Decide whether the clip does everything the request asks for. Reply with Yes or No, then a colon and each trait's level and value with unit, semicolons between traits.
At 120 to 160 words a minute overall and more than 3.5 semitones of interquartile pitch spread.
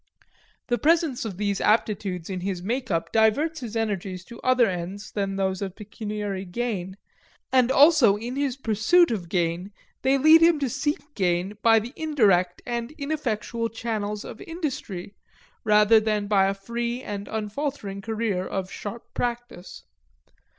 Yes: average, 150 wpm; average, 4.4 semitones